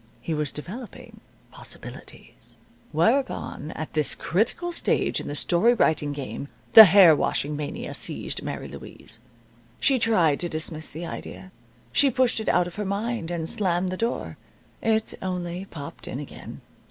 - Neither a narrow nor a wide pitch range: No, wide, 5.9 semitones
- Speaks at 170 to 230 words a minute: No, average, 155 wpm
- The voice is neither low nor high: Yes, medium, 175 Hz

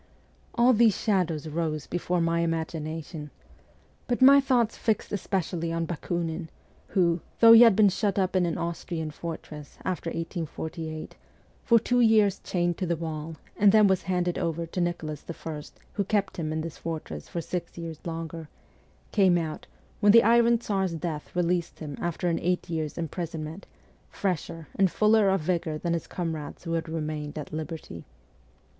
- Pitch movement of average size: Yes, average, 3.2 semitones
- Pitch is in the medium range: Yes, medium, 170 Hz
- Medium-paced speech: Yes, average, 165 wpm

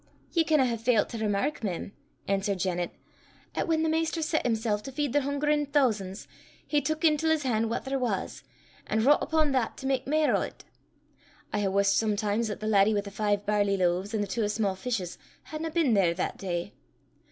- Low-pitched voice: No, high, 225 Hz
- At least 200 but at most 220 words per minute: Yes, fast, 205 wpm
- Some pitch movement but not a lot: No, wide, 6.4 semitones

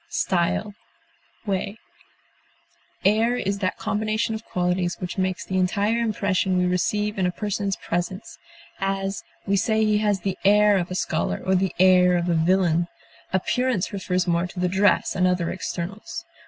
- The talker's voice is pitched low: No, high, 190 Hz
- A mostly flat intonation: Yes, narrow, 2.3 semitones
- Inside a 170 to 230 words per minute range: No, average, 160 wpm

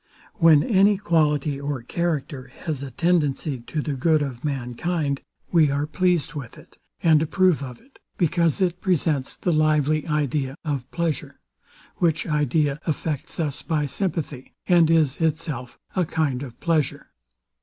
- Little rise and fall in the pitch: No, average, 3.1 semitones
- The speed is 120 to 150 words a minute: Yes, average, 145 wpm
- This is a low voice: No, medium, 150 Hz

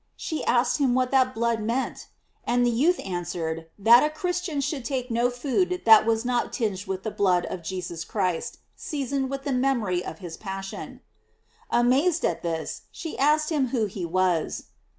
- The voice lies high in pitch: Yes, high, 240 Hz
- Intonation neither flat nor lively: No, wide, 6.4 semitones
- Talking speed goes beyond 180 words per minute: No, average, 175 wpm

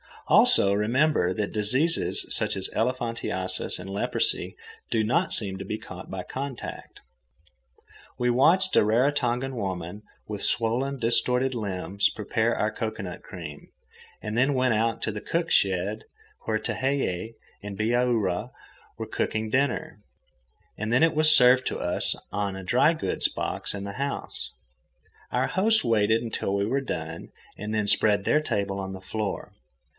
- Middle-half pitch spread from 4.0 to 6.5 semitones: Yes, average, 4.3 semitones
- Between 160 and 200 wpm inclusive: No, average, 150 wpm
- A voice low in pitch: Yes, low, 110 Hz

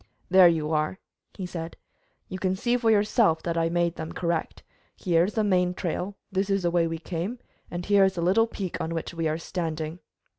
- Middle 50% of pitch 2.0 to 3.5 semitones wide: Yes, average, 2.7 semitones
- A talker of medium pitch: Yes, medium, 175 Hz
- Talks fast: Yes, fast, 220 wpm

